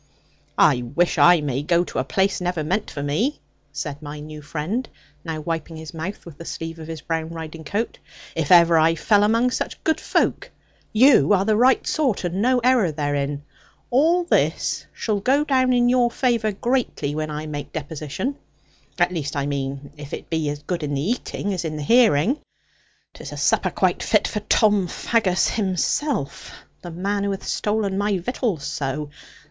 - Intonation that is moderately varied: No, wide, 6.4 semitones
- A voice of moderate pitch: Yes, medium, 175 Hz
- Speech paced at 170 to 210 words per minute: Yes, average, 185 wpm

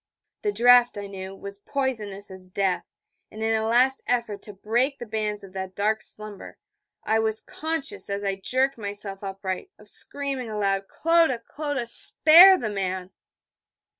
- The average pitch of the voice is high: Yes, high, 215 Hz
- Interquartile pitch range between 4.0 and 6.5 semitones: Yes, average, 4.6 semitones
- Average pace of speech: Yes, average, 160 wpm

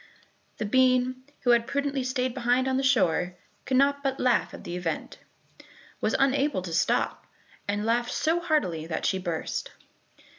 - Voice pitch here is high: Yes, very high, 255 Hz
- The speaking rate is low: No, average, 160 wpm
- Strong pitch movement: Yes, wide, 6.0 semitones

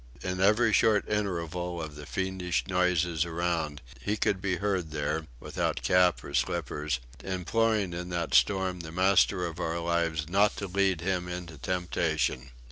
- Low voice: Yes, very low, 90 Hz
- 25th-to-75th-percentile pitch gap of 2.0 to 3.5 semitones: Yes, narrow, 2.6 semitones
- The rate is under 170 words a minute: Yes, average, 155 wpm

